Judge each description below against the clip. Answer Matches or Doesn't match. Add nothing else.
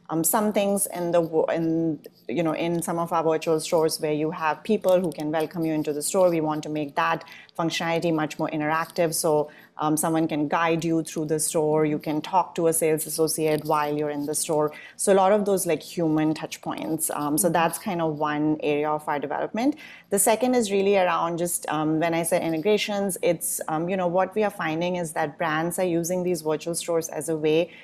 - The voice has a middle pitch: Matches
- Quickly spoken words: Matches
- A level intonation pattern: Matches